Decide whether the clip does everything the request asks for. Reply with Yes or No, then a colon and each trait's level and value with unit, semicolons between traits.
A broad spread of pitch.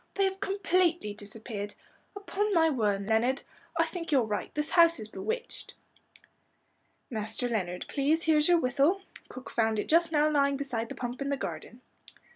Yes: wide, 7.0 semitones